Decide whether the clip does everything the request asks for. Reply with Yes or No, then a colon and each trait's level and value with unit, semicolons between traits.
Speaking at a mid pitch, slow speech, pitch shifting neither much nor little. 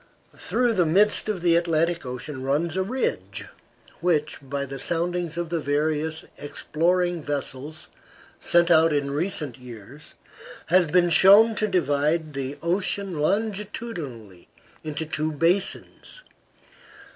Yes: medium, 165 Hz; slow, 120 wpm; average, 3.7 semitones